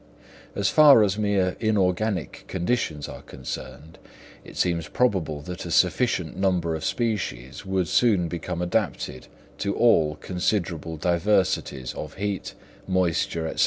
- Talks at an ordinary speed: No, slow, 125 wpm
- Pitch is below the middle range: Yes, very low, 90 Hz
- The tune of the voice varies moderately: Yes, average, 4.0 semitones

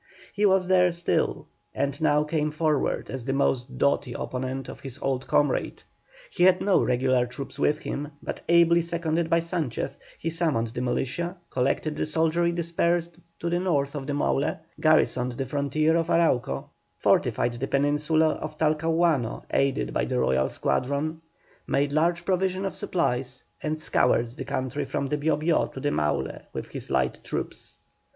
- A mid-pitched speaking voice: Yes, medium, 150 Hz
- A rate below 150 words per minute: No, average, 165 wpm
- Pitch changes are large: No, average, 4.0 semitones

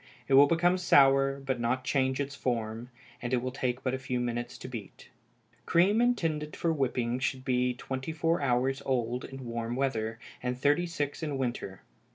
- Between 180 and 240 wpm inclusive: Yes, average, 185 wpm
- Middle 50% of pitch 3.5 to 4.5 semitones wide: No, average, 2.7 semitones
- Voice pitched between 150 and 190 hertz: No, low, 130 Hz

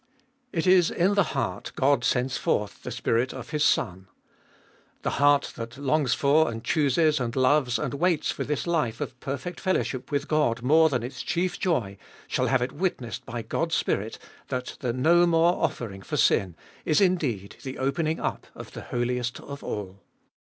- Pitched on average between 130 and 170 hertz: Yes, low, 135 Hz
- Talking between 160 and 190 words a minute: Yes, average, 180 wpm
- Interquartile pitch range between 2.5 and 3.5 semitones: No, average, 4.9 semitones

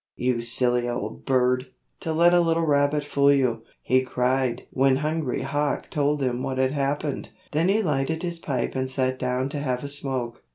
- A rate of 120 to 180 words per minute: No, average, 190 wpm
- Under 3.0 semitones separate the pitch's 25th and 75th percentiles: Yes, narrow, 2.6 semitones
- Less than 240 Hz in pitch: Yes, low, 135 Hz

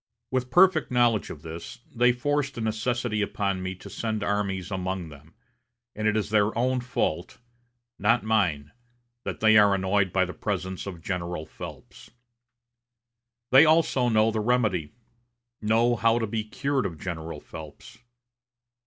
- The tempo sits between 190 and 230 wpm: No, average, 150 wpm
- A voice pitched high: No, low, 105 Hz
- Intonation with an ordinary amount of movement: Yes, average, 4.4 semitones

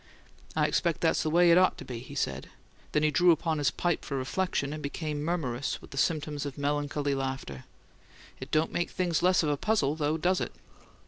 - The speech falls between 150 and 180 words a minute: No, fast, 205 wpm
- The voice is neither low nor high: Yes, medium, 150 Hz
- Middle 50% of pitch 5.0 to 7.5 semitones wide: No, average, 3.3 semitones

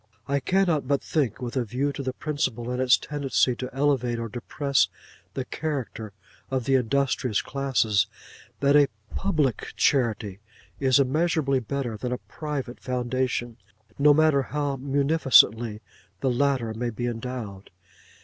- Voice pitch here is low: Yes, low, 130 Hz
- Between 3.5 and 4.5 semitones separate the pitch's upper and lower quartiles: No, average, 2.8 semitones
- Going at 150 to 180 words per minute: No, average, 140 wpm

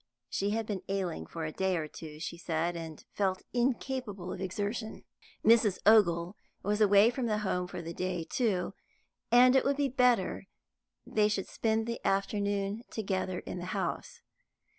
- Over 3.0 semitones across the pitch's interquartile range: Yes, average, 3.7 semitones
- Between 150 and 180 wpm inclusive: Yes, average, 160 wpm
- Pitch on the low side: No, high, 200 Hz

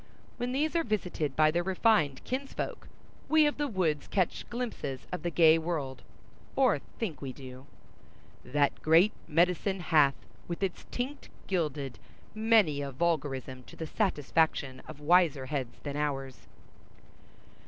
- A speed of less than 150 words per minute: Yes, average, 140 wpm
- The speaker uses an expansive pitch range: Yes, wide, 6.0 semitones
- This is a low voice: No, medium, 160 Hz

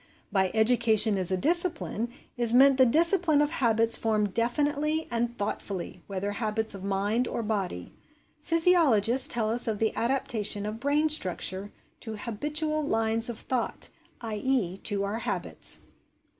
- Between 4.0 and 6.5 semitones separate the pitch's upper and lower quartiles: Yes, average, 4.8 semitones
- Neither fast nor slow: Yes, average, 145 wpm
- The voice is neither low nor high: No, high, 230 Hz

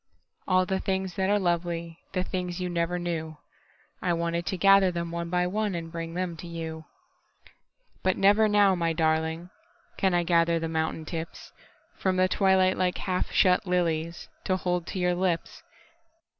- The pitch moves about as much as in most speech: No, narrow, 2.0 semitones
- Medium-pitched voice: Yes, medium, 175 Hz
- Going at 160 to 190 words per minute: No, average, 145 wpm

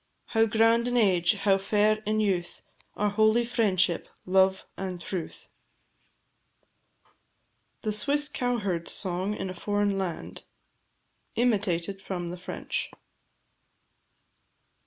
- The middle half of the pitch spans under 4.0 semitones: Yes, average, 3.0 semitones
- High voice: Yes, high, 200 Hz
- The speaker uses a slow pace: Yes, slow, 105 wpm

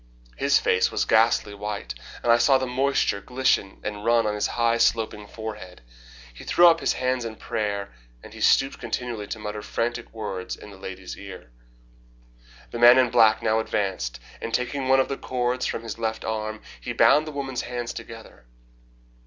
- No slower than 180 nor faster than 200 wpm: Yes, average, 185 wpm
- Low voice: Yes, low, 115 Hz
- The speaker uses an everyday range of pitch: Yes, average, 3.1 semitones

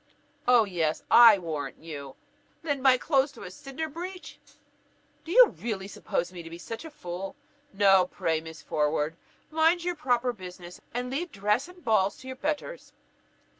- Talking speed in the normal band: Yes, average, 160 wpm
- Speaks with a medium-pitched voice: No, high, 225 Hz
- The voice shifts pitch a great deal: Yes, wide, 8.6 semitones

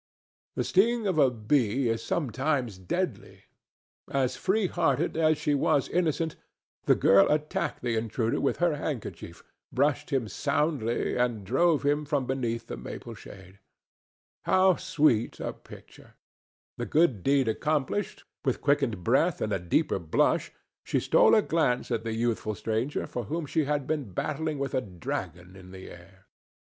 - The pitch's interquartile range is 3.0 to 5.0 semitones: No, wide, 5.5 semitones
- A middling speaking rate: Yes, average, 155 wpm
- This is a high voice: No, low, 135 Hz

